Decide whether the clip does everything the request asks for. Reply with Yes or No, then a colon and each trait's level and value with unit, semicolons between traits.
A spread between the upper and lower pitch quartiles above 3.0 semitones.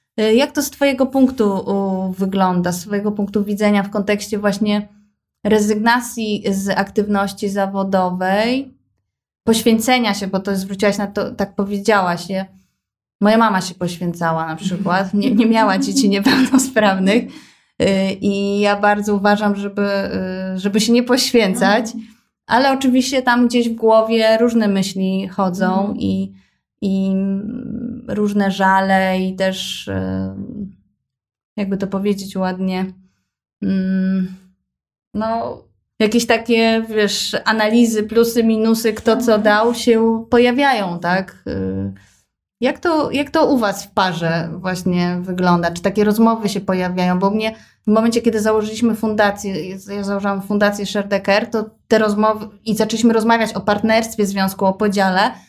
No: average, 2.7 semitones